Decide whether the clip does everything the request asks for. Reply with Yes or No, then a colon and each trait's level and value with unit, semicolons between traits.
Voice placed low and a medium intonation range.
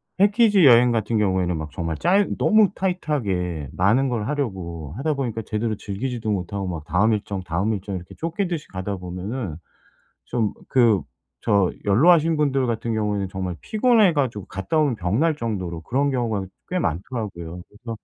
No: low, 110 Hz; wide, 7.0 semitones